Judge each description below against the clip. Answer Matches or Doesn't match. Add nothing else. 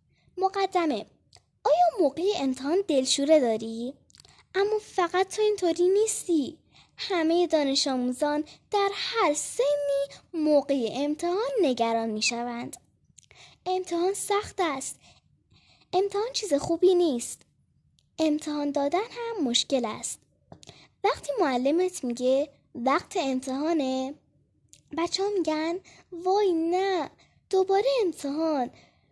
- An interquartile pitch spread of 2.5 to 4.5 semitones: Doesn't match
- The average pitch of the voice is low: Doesn't match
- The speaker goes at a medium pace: Doesn't match